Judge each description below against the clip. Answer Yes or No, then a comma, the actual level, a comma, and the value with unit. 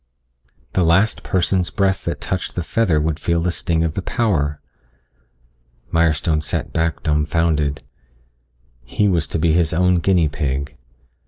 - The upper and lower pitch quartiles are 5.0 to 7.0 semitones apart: No, average, 3.1 semitones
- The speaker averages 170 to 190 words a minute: No, average, 145 wpm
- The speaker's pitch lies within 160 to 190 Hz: No, very low, 80 Hz